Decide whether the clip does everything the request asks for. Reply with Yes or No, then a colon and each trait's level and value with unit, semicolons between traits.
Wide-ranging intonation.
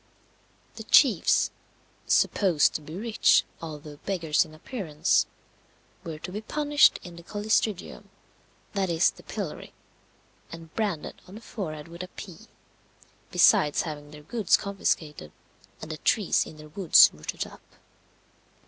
No: average, 4.7 semitones